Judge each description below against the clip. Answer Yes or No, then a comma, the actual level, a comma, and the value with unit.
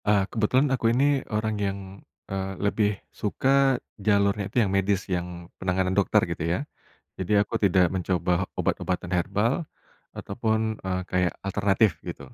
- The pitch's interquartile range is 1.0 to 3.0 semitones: Yes, narrow, 2.5 semitones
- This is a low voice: Yes, low, 100 Hz